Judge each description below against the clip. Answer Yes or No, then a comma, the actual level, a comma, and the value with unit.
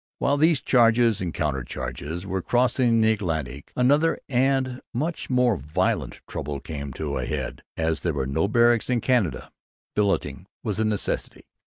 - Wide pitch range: Yes, wide, 8.1 semitones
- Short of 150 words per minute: No, average, 160 wpm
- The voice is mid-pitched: No, low, 105 Hz